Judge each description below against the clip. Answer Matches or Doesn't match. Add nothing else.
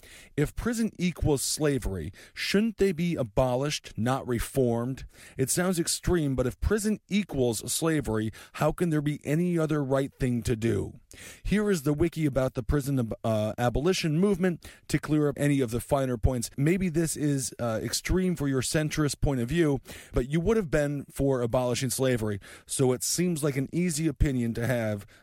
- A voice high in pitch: Doesn't match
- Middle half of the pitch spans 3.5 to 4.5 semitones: Doesn't match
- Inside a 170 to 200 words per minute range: Matches